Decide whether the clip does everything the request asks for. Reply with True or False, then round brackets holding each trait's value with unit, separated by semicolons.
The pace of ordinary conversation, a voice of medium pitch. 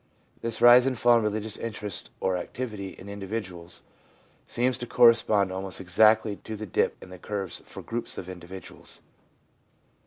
False (155 wpm; 105 Hz)